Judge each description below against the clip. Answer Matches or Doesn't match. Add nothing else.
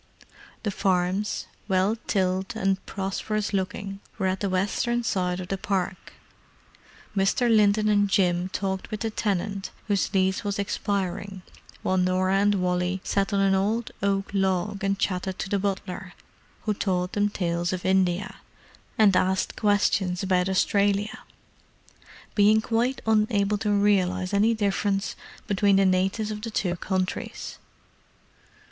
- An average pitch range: Doesn't match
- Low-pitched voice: Doesn't match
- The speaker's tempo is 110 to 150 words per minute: Matches